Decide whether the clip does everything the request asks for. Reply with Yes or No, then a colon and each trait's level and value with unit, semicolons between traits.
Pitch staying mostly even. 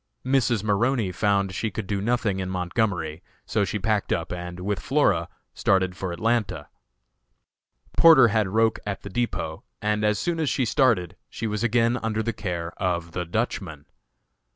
No: average, 3.7 semitones